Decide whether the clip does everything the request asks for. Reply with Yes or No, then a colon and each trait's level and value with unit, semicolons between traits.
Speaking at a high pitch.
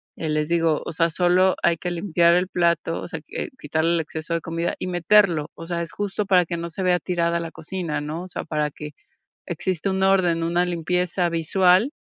No: medium, 170 Hz